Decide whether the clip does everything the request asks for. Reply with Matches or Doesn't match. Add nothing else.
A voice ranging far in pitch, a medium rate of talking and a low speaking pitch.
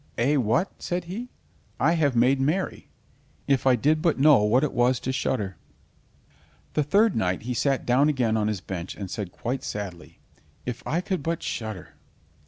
Matches